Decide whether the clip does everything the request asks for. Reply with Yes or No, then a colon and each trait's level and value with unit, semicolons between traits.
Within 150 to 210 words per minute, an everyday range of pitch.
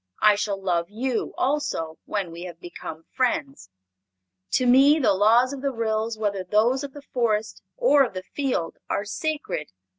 No: average, 170 wpm; wide, 5.8 semitones